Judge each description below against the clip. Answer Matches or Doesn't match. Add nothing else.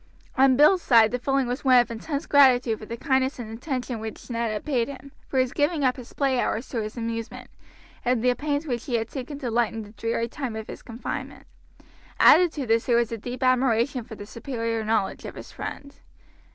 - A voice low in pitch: Doesn't match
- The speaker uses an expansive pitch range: Doesn't match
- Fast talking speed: Matches